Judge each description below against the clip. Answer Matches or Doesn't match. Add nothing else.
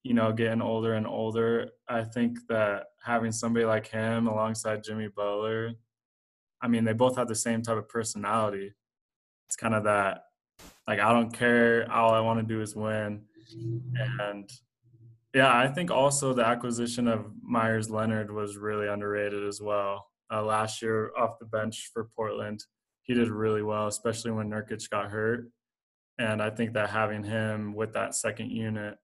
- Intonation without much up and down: Matches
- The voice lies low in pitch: Matches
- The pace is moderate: Matches